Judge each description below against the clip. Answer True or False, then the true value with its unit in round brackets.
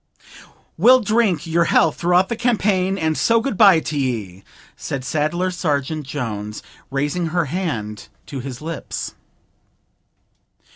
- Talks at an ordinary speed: False (125 wpm)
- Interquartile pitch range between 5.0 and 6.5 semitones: True (5.6 semitones)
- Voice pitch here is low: False (160 Hz)